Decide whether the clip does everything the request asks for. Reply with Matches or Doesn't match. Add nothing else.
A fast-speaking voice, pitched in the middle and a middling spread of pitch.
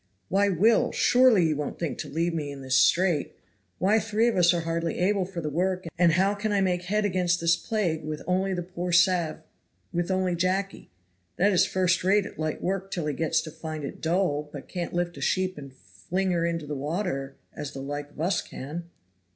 Matches